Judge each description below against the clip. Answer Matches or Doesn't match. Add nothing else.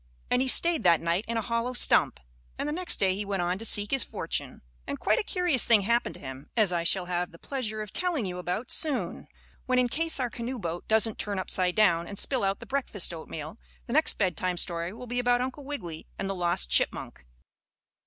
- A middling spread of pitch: Doesn't match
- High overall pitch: Matches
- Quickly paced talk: Matches